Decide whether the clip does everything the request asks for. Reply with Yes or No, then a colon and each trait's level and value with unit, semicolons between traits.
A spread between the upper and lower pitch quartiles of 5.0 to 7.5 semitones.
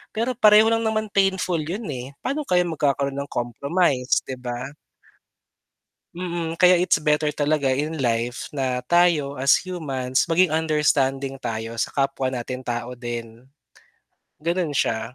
Yes: wide, 5.5 semitones